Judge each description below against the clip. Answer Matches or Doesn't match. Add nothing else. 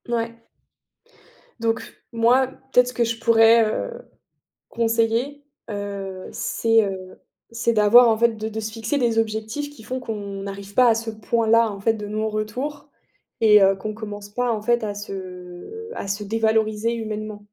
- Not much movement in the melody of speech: Matches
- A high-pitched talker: Matches